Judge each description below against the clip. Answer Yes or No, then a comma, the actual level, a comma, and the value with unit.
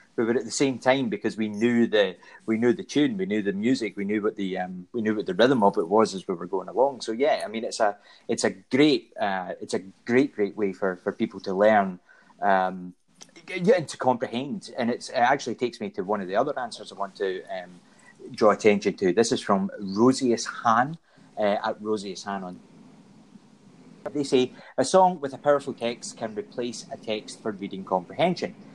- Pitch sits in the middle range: No, low, 115 Hz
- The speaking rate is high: Yes, fast, 215 wpm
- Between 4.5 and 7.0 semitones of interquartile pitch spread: Yes, average, 4.9 semitones